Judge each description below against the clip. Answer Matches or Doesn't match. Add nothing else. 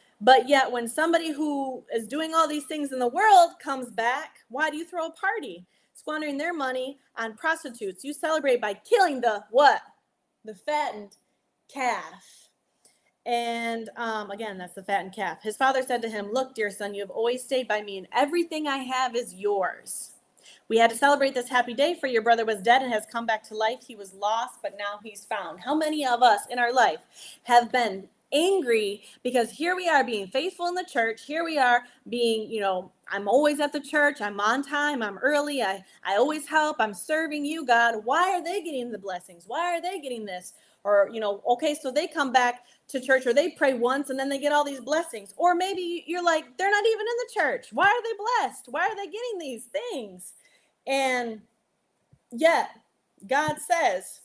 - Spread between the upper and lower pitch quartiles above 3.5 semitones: Matches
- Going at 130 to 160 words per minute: Doesn't match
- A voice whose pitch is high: Matches